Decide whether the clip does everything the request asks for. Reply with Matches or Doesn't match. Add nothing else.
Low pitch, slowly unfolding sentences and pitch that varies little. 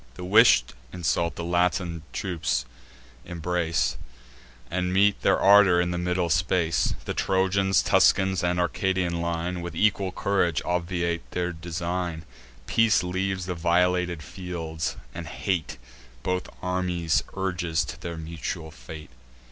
Matches